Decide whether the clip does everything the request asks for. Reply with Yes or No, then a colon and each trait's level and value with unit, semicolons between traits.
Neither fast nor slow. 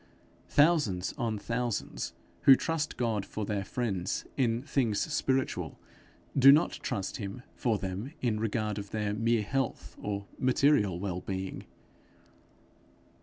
No: slow, 125 wpm